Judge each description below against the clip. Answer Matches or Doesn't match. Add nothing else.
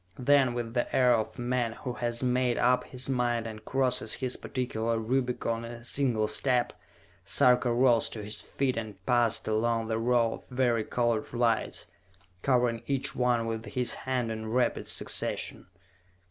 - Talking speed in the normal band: Matches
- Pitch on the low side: Matches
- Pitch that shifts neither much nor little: Doesn't match